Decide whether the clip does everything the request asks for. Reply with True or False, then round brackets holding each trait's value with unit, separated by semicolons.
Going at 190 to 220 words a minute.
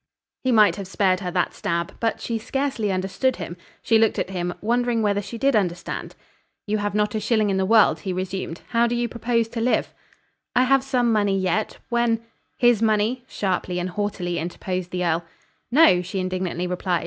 True (195 wpm)